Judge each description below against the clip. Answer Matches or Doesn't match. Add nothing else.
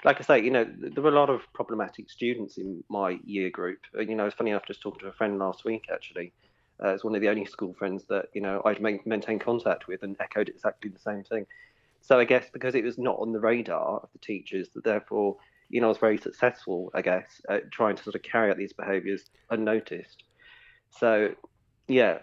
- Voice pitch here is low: Matches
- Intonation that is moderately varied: Doesn't match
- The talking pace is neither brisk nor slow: Doesn't match